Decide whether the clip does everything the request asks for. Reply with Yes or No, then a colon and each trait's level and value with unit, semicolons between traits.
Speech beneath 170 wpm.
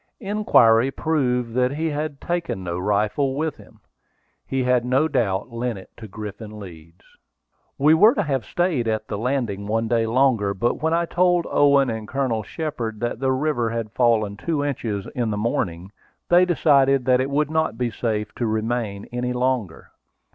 No: average, 175 wpm